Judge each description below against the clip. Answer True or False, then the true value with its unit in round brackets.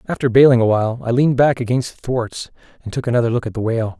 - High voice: False (120 Hz)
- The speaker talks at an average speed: False (240 wpm)